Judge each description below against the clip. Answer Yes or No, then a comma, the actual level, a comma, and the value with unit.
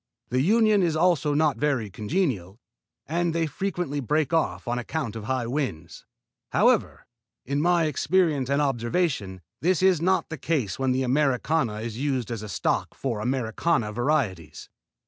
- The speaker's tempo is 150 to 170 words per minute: Yes, average, 155 wpm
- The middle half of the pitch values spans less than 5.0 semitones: No, wide, 5.6 semitones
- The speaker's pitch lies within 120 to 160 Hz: Yes, medium, 140 Hz